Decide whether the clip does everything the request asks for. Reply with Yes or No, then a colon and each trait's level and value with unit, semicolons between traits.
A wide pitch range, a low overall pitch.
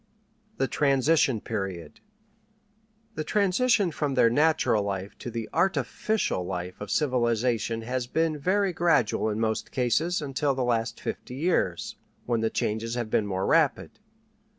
Yes: wide, 6.1 semitones; low, 125 Hz